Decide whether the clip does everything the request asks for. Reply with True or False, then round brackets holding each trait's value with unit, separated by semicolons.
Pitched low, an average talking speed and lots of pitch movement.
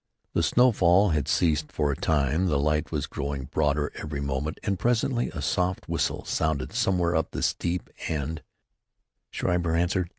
False (80 Hz; 160 wpm; 3.4 semitones)